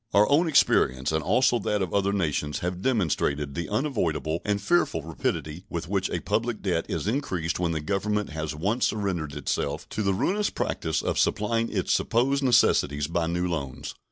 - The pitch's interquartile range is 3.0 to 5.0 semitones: No, wide, 5.5 semitones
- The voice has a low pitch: Yes, very low, 95 Hz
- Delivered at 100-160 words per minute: No, average, 180 wpm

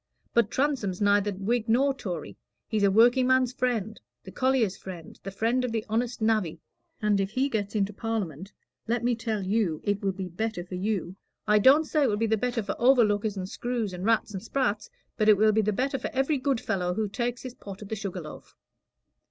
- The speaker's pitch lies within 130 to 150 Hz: No, high, 220 Hz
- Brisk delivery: Yes, fast, 215 wpm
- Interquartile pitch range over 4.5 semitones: No, average, 3.6 semitones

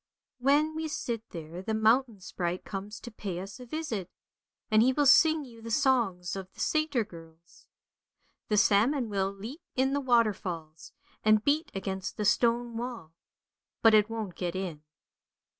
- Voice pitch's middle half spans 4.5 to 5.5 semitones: Yes, average, 5.1 semitones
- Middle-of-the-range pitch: No, high, 220 Hz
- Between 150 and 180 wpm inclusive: Yes, average, 160 wpm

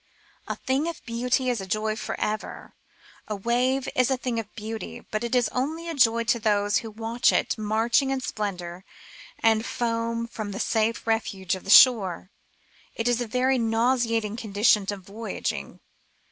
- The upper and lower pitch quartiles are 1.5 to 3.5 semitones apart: Yes, narrow, 2.6 semitones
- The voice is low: No, high, 230 Hz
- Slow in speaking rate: No, average, 175 wpm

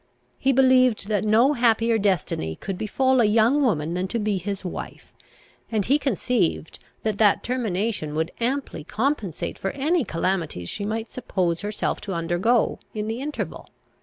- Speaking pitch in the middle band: No, high, 215 Hz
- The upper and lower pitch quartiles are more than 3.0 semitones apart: Yes, average, 5.0 semitones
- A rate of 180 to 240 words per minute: No, average, 160 wpm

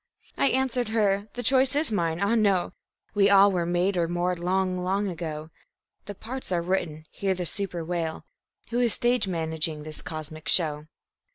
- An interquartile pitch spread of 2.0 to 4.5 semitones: Yes, average, 3.8 semitones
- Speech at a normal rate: Yes, average, 175 wpm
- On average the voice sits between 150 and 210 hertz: Yes, medium, 185 Hz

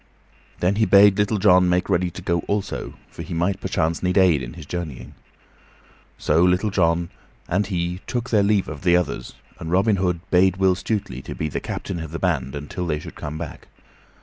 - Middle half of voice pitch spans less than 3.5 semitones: Yes, average, 2.7 semitones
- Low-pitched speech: Yes, very low, 90 Hz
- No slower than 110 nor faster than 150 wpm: No, average, 200 wpm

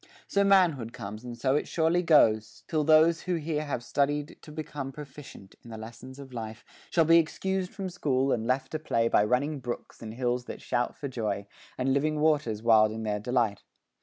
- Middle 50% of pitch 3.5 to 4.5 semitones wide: No, average, 5.0 semitones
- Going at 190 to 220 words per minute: Yes, fast, 205 wpm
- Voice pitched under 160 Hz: Yes, low, 135 Hz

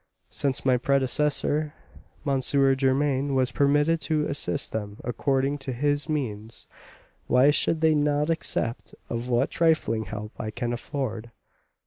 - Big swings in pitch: No, average, 3.3 semitones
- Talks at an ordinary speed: No, slow, 130 wpm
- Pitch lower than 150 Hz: Yes, low, 135 Hz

